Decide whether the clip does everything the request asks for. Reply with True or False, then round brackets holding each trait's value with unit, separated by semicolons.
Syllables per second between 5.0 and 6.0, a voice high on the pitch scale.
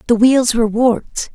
True (5.2 syllables/s; 235 Hz)